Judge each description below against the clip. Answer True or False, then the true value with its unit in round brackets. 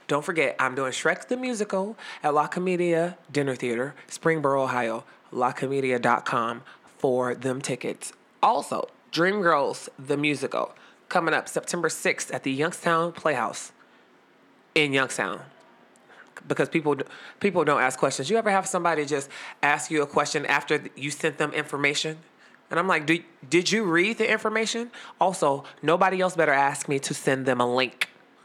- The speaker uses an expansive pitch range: False (4.2 semitones)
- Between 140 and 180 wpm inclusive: True (150 wpm)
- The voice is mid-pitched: True (150 Hz)